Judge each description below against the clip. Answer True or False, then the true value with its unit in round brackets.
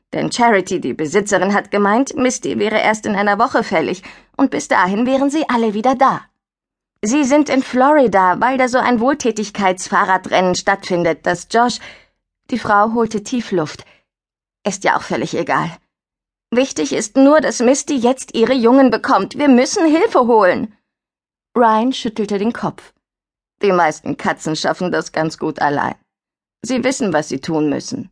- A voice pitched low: False (230 Hz)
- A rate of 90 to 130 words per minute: False (155 wpm)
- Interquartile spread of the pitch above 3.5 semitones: True (4.8 semitones)